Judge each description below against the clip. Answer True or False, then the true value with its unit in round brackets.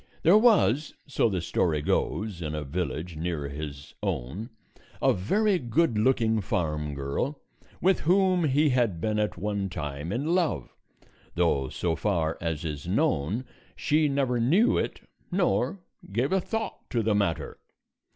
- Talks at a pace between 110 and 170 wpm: True (150 wpm)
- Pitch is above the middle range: False (105 Hz)